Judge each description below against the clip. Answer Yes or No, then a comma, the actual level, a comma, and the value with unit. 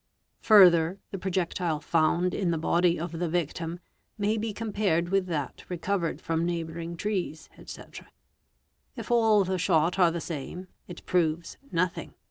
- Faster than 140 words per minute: Yes, average, 155 wpm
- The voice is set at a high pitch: No, medium, 175 Hz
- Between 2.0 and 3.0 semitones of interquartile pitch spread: Yes, narrow, 2.4 semitones